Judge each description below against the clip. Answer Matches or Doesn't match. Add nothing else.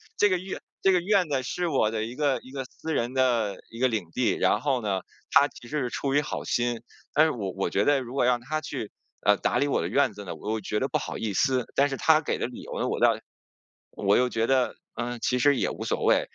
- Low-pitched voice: Matches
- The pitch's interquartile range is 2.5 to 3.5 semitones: Doesn't match